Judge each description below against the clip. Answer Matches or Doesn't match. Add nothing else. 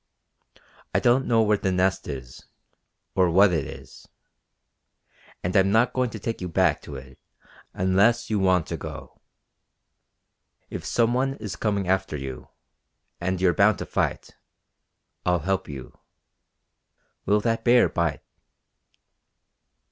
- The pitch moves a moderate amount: Matches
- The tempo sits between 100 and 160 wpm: Matches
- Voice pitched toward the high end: Doesn't match